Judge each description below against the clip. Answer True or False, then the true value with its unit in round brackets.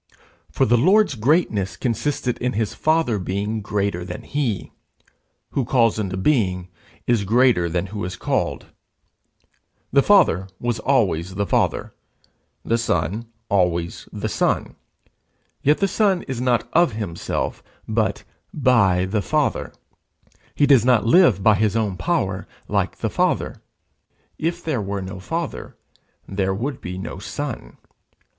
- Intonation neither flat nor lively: False (5.7 semitones)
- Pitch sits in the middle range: False (110 Hz)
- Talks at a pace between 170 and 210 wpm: False (135 wpm)